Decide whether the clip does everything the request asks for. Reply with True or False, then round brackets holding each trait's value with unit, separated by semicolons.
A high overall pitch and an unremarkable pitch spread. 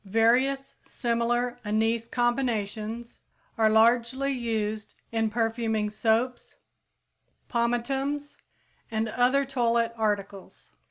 False (235 Hz; 2.0 semitones)